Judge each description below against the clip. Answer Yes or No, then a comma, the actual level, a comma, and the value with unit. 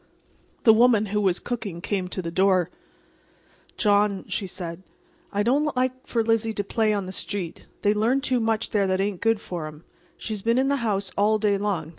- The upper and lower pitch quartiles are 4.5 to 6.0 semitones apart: No, average, 3.0 semitones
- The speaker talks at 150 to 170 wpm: No, average, 200 wpm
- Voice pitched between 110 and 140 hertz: No, high, 205 Hz